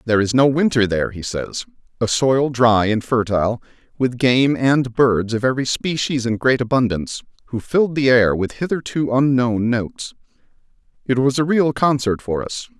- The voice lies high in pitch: No, low, 125 Hz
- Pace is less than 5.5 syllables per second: Yes, 5.0 syllables/s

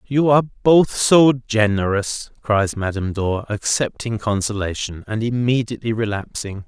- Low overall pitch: Yes, low, 110 Hz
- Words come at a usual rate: No, slow, 115 wpm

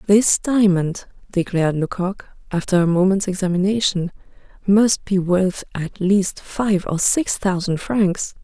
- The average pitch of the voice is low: No, high, 190 Hz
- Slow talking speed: Yes, slow, 130 wpm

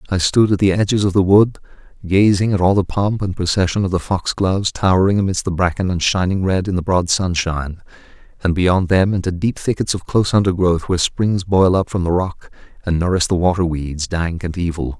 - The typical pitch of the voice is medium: No, very low, 90 Hz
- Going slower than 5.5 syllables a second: No, 5.6 syllables/s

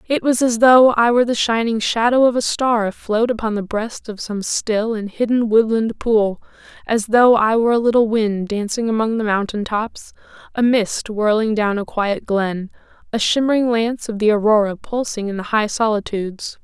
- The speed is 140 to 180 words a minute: No, average, 190 wpm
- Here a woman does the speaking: Yes, female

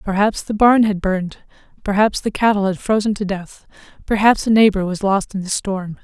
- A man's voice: No, female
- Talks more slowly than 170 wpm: No, average, 200 wpm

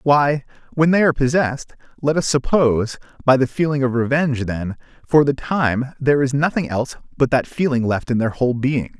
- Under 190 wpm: No, average, 195 wpm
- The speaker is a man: Yes, male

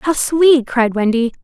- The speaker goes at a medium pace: Yes, average, 170 wpm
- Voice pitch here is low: No, very high, 260 Hz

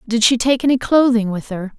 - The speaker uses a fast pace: Yes, fast, 235 wpm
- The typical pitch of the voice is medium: No, high, 235 Hz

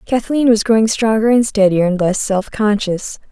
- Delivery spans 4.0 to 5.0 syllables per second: Yes, 4.8 syllables/s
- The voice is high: Yes, high, 215 Hz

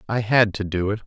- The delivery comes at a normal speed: No, fast, 280 wpm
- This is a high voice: No, low, 105 Hz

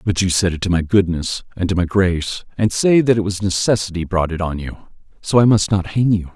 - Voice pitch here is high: No, very low, 95 Hz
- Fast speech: Yes, fast, 255 wpm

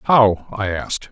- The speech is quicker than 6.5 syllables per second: No, 4.0 syllables/s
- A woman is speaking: No, male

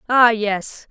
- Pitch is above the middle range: Yes, high, 220 Hz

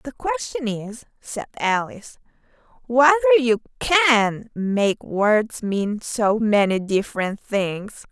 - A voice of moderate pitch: No, high, 230 Hz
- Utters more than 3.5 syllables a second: No, 3.3 syllables/s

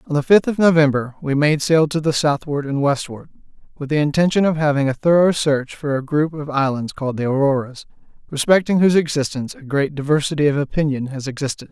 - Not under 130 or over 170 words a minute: No, average, 200 wpm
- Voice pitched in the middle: Yes, medium, 145 Hz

